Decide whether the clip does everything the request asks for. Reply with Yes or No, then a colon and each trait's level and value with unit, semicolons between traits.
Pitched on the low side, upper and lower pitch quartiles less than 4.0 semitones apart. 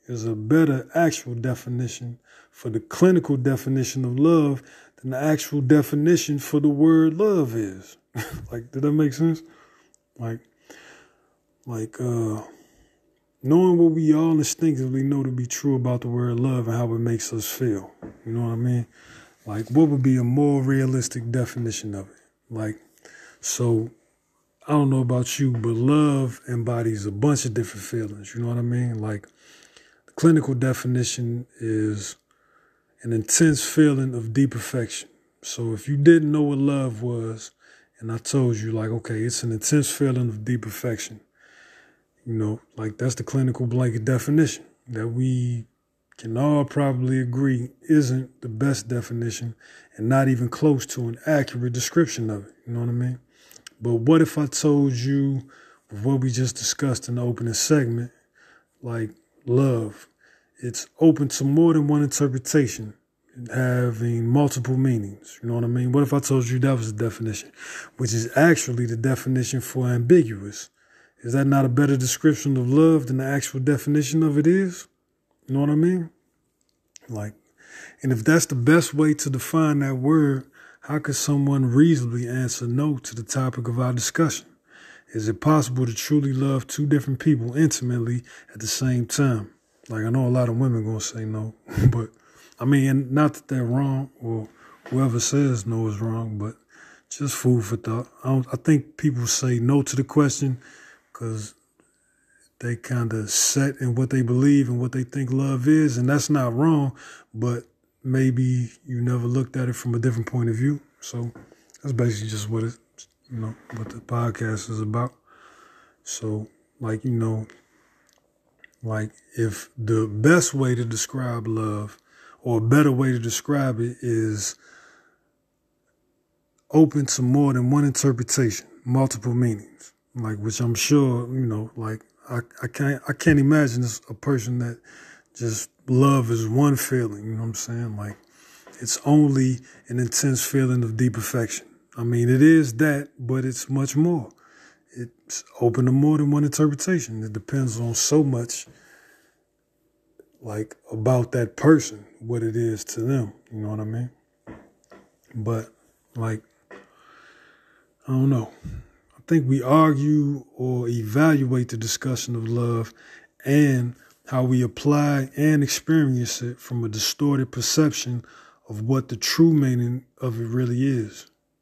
Yes: low, 125 Hz; average, 3.4 semitones